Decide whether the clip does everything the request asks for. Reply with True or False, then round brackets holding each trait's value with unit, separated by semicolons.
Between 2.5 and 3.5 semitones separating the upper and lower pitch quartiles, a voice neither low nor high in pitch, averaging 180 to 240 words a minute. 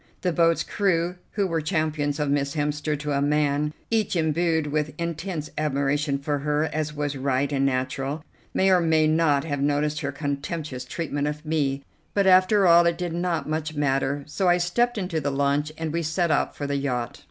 True (2.8 semitones; 150 Hz; 195 wpm)